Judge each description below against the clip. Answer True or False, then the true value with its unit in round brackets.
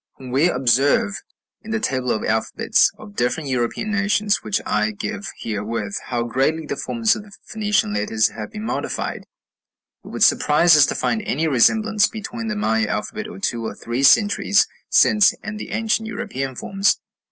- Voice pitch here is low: False (150 Hz)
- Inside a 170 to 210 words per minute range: True (175 wpm)